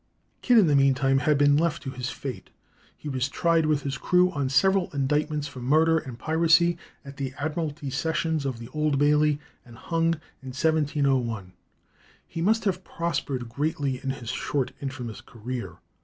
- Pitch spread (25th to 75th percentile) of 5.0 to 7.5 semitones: No, average, 3.5 semitones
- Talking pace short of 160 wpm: No, average, 170 wpm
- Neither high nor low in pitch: Yes, medium, 145 Hz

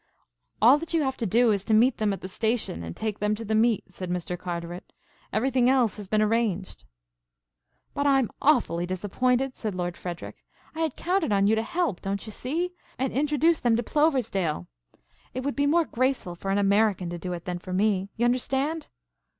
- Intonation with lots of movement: Yes, wide, 5.9 semitones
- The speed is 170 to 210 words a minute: Yes, average, 200 wpm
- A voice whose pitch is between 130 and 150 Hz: No, high, 220 Hz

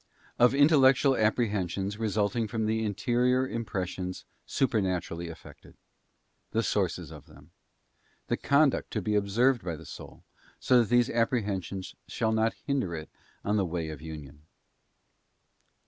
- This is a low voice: Yes, low, 105 Hz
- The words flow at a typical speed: No, slow, 130 wpm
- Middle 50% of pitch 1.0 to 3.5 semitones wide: No, average, 4.9 semitones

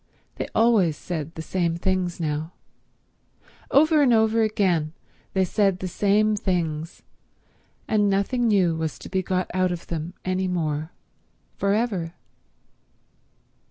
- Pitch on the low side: No, medium, 185 Hz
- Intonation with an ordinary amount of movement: Yes, average, 3.9 semitones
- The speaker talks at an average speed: No, slow, 125 wpm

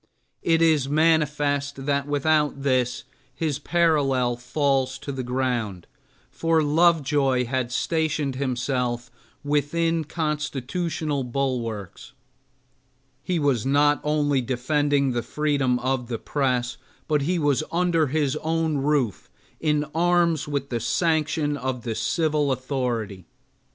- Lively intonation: No, average, 3.2 semitones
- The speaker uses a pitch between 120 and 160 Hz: Yes, medium, 140 Hz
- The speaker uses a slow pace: Yes, slow, 115 wpm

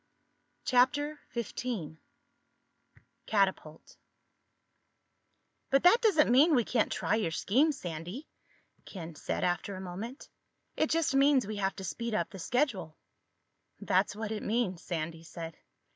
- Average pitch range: No, wide, 7.3 semitones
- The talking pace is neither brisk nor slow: No, slow, 130 wpm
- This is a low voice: No, high, 215 Hz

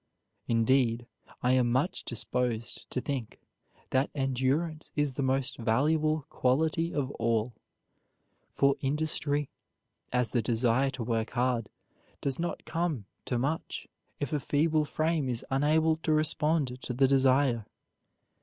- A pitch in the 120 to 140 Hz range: Yes, low, 135 Hz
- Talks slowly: Yes, slow, 130 wpm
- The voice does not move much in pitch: No, average, 3.7 semitones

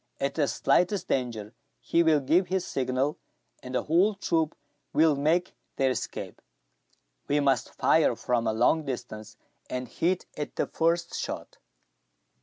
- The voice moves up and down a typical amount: Yes, average, 4.8 semitones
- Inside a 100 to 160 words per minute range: Yes, average, 145 wpm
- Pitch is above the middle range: No, medium, 145 Hz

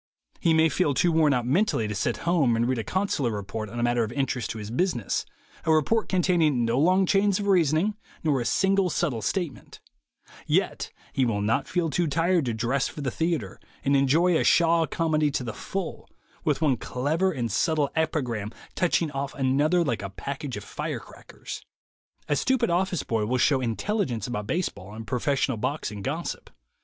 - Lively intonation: Yes, wide, 6.2 semitones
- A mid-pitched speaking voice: Yes, medium, 145 Hz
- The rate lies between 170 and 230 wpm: Yes, average, 190 wpm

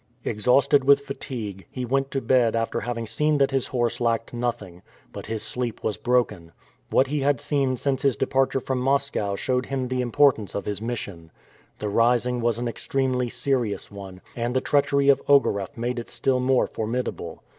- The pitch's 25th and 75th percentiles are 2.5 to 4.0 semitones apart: Yes, average, 2.9 semitones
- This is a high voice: No, low, 125 Hz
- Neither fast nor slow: Yes, average, 180 wpm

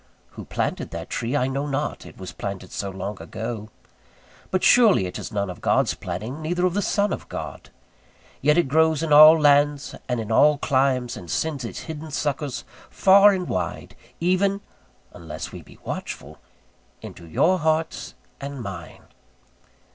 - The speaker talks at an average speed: Yes, average, 165 wpm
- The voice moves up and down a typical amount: No, wide, 6.5 semitones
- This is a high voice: No, medium, 145 Hz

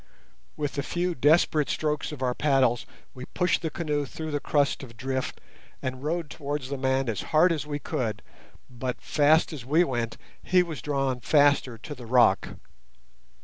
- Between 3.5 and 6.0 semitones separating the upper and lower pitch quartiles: No, average, 3.1 semitones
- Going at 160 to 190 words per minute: Yes, average, 175 wpm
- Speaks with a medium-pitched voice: Yes, medium, 145 Hz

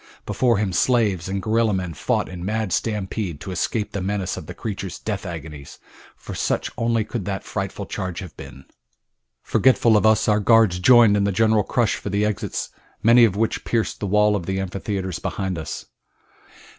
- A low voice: Yes, low, 100 Hz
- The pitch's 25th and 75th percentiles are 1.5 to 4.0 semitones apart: Yes, average, 2.8 semitones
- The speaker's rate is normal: Yes, average, 185 wpm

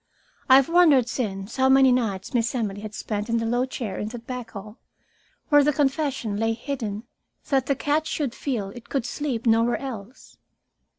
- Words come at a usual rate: Yes, average, 185 wpm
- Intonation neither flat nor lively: Yes, average, 3.6 semitones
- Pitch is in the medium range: No, high, 240 Hz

